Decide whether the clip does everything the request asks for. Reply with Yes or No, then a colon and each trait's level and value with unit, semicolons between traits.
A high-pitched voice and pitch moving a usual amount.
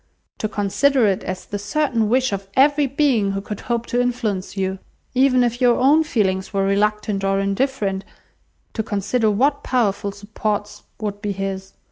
Yes: high, 210 Hz; average, 4.1 semitones